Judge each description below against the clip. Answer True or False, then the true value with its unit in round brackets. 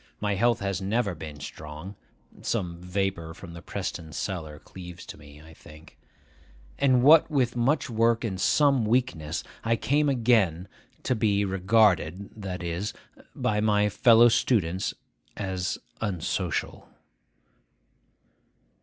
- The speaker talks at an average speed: False (120 wpm)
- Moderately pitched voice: False (100 Hz)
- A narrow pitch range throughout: False (5.2 semitones)